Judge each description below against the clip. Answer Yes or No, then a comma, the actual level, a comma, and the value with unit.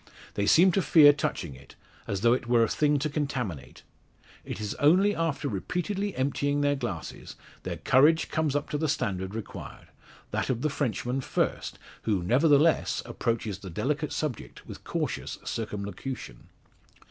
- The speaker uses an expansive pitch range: Yes, wide, 6.1 semitones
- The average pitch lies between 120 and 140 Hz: Yes, low, 135 Hz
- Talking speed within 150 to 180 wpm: Yes, average, 155 wpm